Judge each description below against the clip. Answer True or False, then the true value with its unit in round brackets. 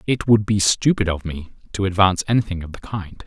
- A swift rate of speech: True (220 wpm)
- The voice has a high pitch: False (95 Hz)